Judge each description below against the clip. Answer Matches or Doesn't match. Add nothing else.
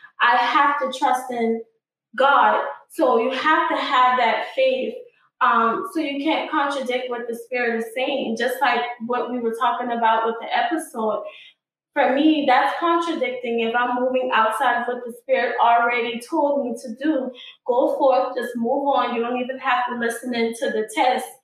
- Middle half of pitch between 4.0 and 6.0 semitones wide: Doesn't match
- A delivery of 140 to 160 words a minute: Doesn't match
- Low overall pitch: Doesn't match